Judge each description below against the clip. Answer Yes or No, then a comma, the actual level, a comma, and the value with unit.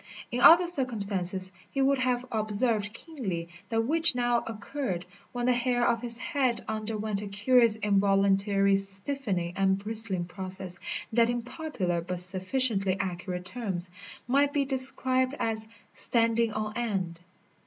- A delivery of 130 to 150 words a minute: Yes, slow, 135 wpm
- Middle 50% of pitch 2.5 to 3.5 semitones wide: No, average, 4.4 semitones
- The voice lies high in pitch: Yes, high, 220 Hz